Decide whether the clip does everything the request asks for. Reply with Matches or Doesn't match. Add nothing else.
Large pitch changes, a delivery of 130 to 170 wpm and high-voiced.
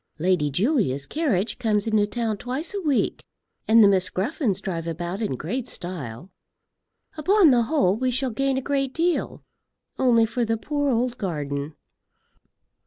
Matches